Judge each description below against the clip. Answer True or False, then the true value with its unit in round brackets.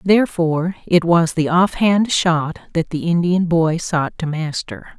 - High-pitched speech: False (170 Hz)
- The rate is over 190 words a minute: False (170 wpm)